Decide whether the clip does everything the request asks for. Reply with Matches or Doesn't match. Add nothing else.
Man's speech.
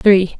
Doesn't match